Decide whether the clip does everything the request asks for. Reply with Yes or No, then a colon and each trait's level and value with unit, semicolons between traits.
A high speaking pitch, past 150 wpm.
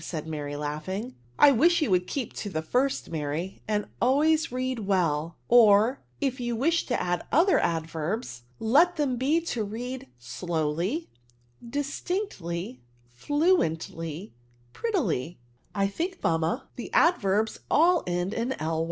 No: high, 215 Hz; average, 145 wpm